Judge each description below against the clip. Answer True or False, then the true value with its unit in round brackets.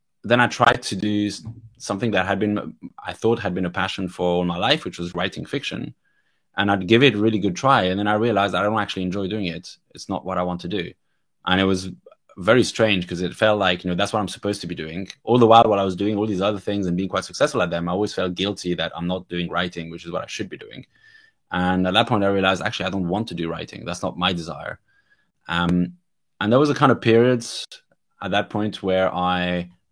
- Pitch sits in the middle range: False (95 Hz)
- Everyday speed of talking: False (260 wpm)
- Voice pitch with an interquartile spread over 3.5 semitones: False (2.9 semitones)